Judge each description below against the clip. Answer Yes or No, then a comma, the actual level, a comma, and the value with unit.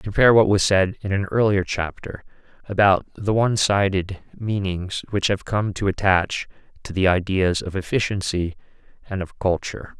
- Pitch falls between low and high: No, very low, 95 Hz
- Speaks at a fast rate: No, average, 155 wpm